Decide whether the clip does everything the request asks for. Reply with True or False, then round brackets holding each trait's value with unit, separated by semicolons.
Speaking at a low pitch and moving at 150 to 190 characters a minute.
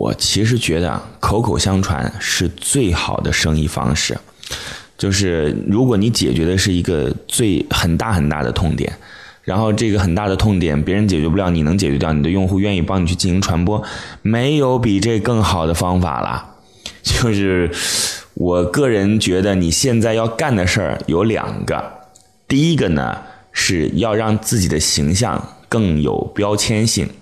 False (95 Hz; 250 characters per minute)